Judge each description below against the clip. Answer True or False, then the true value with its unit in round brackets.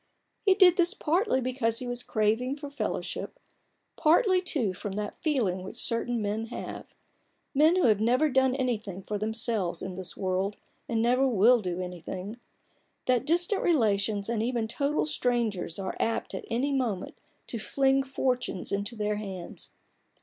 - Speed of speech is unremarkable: True (160 wpm)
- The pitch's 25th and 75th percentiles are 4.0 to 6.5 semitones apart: True (4.8 semitones)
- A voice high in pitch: True (235 Hz)